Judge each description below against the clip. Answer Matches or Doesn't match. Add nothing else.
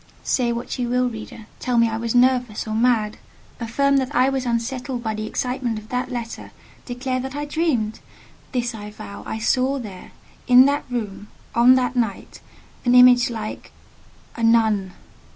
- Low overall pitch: Doesn't match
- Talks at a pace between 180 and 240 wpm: Doesn't match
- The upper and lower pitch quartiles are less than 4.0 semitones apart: Matches